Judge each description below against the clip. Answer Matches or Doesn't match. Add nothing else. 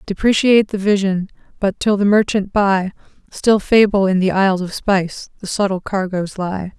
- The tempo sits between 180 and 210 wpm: Doesn't match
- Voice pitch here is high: Matches